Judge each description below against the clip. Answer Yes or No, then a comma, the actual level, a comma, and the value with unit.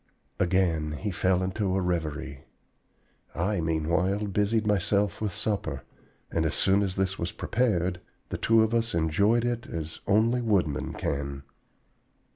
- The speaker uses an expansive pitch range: No, average, 4.1 semitones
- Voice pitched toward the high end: No, very low, 95 Hz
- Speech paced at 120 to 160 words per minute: Yes, average, 140 wpm